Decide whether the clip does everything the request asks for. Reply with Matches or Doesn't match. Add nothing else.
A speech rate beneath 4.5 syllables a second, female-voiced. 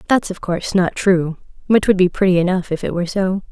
Doesn't match